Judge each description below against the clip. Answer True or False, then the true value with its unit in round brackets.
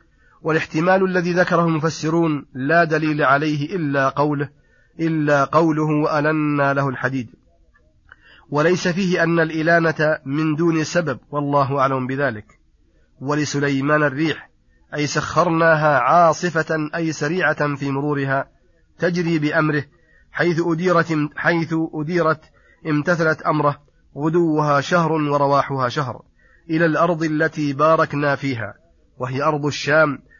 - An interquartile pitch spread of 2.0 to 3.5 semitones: True (2.5 semitones)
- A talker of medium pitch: True (155 Hz)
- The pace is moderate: True (105 wpm)